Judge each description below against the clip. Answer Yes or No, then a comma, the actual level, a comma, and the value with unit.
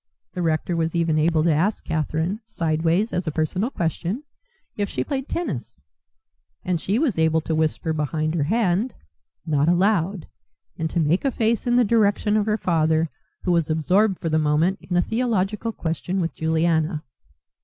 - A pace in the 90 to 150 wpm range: No, average, 175 wpm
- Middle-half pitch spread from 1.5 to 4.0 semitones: No, average, 4.5 semitones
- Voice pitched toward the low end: No, medium, 170 Hz